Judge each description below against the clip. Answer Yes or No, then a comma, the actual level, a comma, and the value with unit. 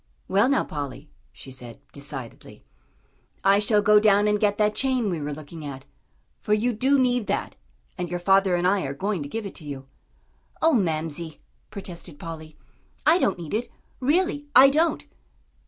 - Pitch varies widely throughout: Yes, wide, 6.3 semitones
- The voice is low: No, high, 195 Hz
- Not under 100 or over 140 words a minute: No, average, 175 wpm